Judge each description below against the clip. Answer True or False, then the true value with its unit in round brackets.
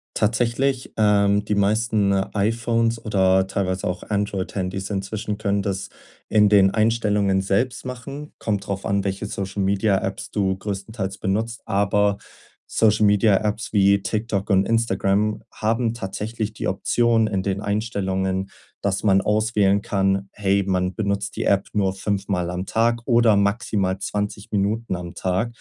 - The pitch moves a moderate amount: False (2.1 semitones)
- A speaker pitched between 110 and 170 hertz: False (100 Hz)